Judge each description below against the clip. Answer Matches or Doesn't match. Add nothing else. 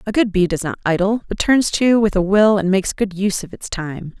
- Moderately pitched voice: Doesn't match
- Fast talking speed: Matches